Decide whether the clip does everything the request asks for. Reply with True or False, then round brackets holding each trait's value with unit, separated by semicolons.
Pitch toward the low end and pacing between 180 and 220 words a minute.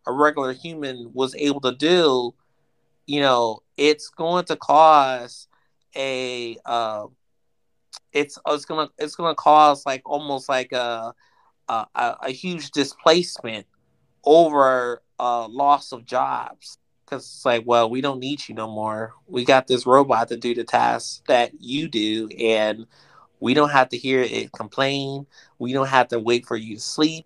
False (130 Hz; 160 wpm)